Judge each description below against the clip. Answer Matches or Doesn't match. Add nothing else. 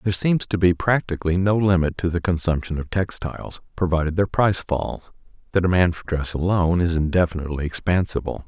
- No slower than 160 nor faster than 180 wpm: Matches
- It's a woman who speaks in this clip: Doesn't match